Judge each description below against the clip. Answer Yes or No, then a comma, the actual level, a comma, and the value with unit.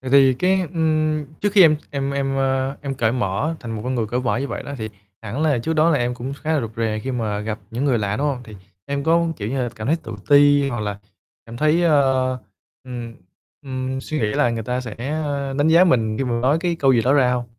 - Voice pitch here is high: No, low, 130 Hz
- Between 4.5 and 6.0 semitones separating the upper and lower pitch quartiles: No, average, 4.0 semitones